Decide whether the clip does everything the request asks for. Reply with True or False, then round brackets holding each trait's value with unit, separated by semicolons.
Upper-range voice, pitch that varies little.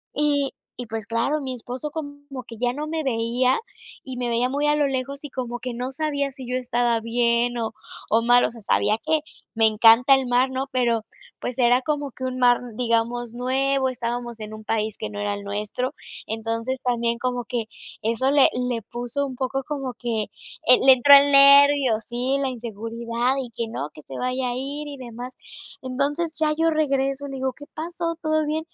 False (250 Hz; 3.0 semitones)